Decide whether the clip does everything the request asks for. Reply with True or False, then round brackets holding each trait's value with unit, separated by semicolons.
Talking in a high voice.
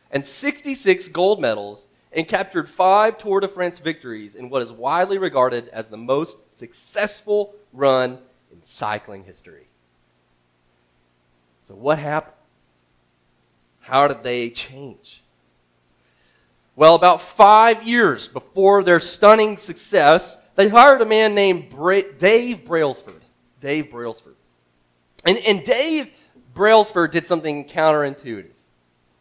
False (140 Hz)